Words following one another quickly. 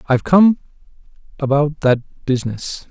No: slow, 85 wpm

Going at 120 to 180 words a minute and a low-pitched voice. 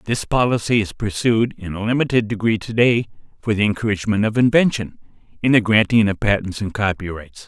Yes: average, 175 wpm; low, 110 Hz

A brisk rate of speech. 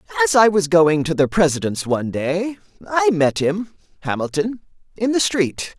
No: average, 165 wpm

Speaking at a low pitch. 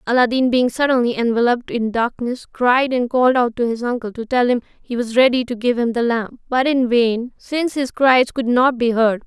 No: high, 245 Hz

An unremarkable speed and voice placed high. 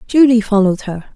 Yes: average, 155 wpm; high, 220 Hz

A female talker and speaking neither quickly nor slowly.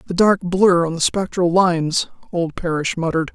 Yes: female; average, 180 wpm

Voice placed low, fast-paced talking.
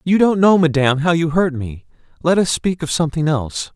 No: medium, 160 Hz; fast, 225 wpm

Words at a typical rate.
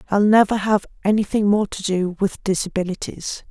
Yes: average, 155 wpm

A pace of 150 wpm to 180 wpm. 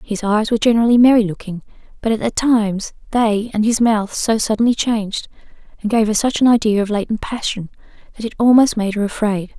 No: average, 195 wpm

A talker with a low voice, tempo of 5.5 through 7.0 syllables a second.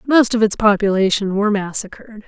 No: high, 210 Hz; 5.7 syllables/s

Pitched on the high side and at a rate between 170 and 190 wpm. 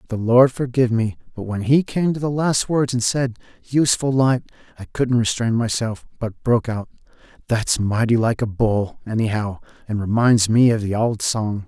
No: low, 115 Hz; average, 185 wpm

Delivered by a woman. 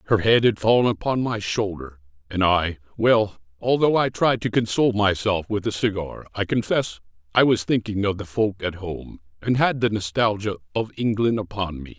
No: male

